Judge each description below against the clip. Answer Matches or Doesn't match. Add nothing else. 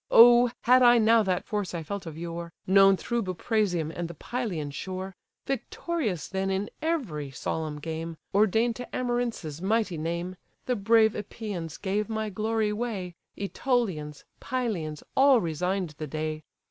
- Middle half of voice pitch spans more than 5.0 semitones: Matches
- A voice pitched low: Doesn't match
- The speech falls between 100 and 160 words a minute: Matches